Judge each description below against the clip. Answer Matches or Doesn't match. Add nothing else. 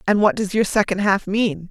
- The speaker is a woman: Matches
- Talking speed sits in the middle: Doesn't match